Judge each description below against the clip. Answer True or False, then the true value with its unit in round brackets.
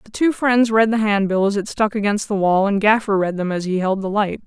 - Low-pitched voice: False (205 Hz)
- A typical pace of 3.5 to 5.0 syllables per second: False (5.6 syllables/s)